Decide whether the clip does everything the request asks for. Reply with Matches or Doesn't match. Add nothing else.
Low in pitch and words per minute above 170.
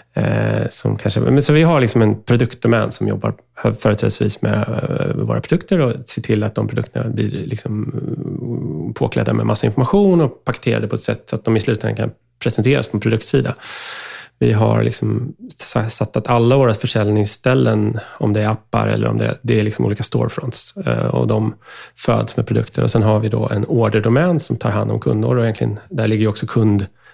Matches